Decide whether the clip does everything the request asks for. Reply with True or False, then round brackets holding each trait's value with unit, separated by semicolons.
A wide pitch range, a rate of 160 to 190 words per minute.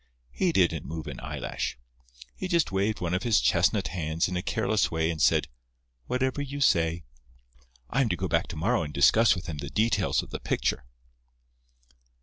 True (6.1 semitones; 185 wpm)